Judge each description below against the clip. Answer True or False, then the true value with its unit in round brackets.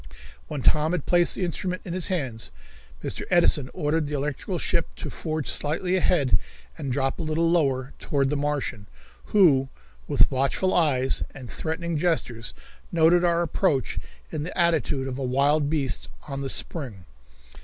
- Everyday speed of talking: True (160 wpm)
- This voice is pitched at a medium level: True (150 Hz)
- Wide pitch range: False (4.1 semitones)